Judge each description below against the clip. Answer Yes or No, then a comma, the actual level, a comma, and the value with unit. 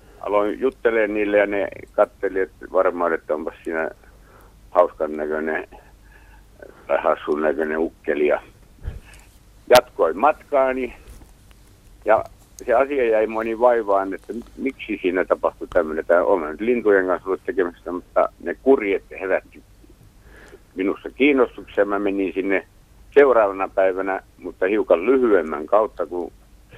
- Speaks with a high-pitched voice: No, low, 100 Hz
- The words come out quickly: No, average, 120 wpm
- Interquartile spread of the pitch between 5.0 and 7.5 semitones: No, narrow, 2.5 semitones